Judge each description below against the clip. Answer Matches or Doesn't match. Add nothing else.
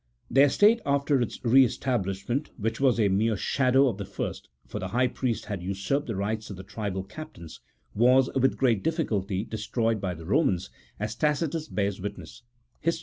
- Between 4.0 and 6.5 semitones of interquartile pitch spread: Matches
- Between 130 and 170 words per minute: Doesn't match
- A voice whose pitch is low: Matches